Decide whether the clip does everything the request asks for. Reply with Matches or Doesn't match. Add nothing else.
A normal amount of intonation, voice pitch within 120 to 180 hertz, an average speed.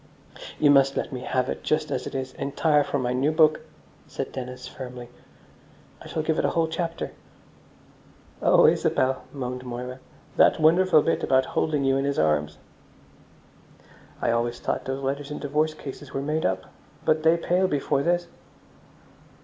Matches